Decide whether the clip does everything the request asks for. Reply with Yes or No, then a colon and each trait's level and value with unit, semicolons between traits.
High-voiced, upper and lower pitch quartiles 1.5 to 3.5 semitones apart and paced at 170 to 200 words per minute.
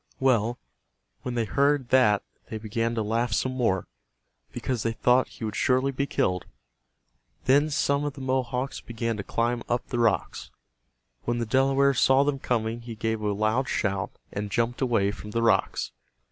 No: low, 120 Hz; average, 3.0 semitones; average, 175 wpm